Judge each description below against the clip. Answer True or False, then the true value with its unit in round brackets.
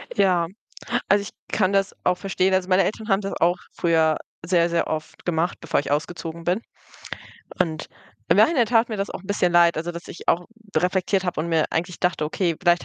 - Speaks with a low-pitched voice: False (175 Hz)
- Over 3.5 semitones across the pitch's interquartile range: False (2.6 semitones)